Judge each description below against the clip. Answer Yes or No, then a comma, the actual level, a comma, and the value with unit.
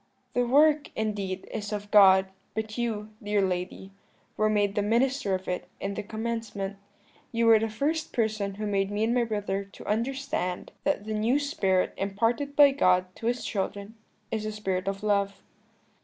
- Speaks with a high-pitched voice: Yes, high, 210 Hz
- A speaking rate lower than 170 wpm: No, average, 175 wpm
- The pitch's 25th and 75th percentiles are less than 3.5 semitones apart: Yes, average, 2.8 semitones